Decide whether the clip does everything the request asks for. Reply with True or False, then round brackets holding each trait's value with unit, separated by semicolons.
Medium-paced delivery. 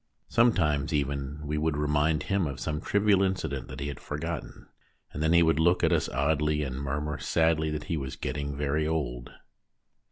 False (210 wpm)